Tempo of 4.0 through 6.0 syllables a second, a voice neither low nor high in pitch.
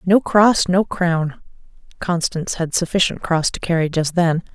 Yes: 4.5 syllables/s; medium, 175 Hz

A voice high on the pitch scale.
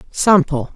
No: medium, 165 Hz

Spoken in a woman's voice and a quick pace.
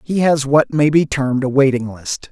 No: male; fast, 235 wpm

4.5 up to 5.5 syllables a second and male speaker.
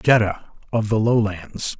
No: 4.1 syllables/s; male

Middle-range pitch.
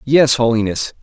No: low, 120 Hz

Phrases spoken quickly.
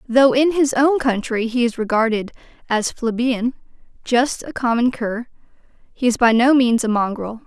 No: average, 170 wpm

